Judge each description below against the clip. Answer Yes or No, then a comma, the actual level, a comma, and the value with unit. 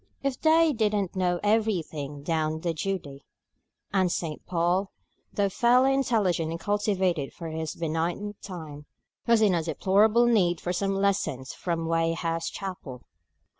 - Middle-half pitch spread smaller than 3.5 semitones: No, average, 4.0 semitones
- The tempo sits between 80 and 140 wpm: Yes, slow, 135 wpm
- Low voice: No, medium, 180 Hz